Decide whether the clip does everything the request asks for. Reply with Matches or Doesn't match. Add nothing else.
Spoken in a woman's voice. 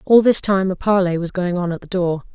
Matches